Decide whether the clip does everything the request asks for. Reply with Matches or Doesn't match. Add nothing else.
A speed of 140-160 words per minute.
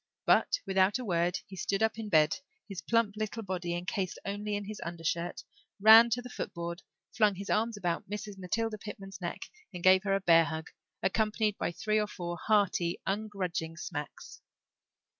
Doesn't match